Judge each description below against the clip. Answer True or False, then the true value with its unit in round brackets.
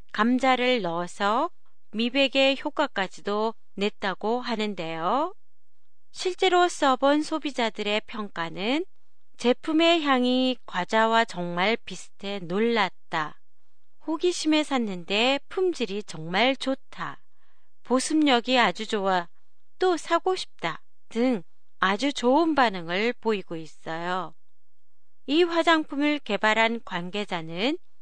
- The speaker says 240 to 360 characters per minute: False (220 characters per minute)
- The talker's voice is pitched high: True (235 Hz)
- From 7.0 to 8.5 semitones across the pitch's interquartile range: False (6.5 semitones)